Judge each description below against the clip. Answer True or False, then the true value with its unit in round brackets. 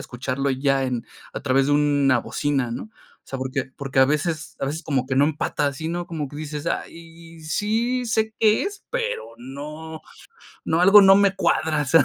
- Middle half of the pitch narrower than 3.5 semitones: False (4.0 semitones)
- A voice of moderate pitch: True (150 Hz)